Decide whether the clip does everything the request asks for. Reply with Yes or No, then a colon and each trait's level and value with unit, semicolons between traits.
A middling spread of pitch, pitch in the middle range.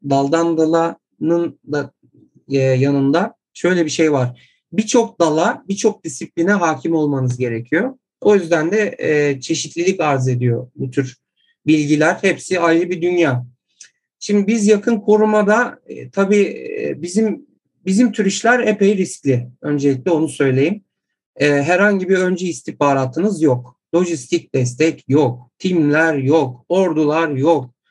No: wide, 5.7 semitones; medium, 165 Hz